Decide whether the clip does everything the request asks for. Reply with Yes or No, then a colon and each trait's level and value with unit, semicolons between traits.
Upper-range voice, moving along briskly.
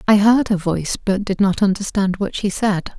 Yes: high, 200 Hz; fast, 220 wpm